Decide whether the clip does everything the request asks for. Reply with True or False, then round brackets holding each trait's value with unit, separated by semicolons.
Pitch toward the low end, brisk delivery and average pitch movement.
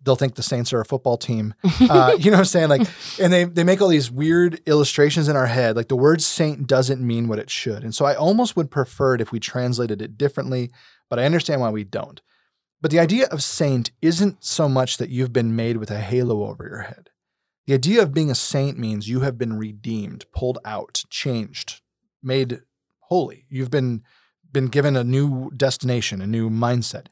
True (130 Hz; 215 wpm; 4.3 semitones)